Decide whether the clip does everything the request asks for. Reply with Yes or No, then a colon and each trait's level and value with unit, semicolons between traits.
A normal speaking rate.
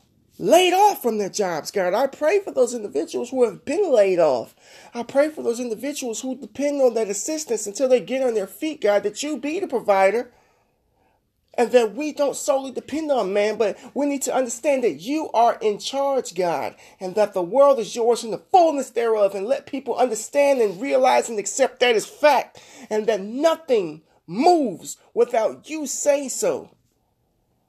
Yes: average, 185 wpm